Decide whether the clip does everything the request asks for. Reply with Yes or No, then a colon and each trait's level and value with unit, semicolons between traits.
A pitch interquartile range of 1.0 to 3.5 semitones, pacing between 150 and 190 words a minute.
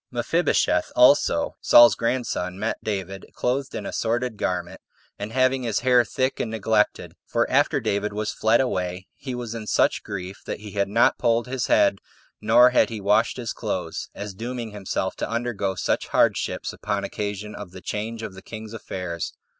Yes: average, 3.2 semitones; average, 180 wpm